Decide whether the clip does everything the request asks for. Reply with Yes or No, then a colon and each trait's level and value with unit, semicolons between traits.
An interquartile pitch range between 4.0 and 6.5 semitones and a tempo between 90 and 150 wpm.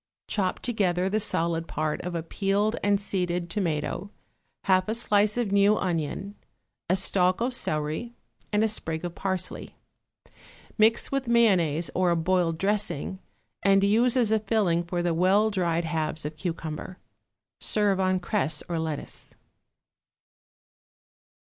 No: average, 3.6 semitones; average, 140 wpm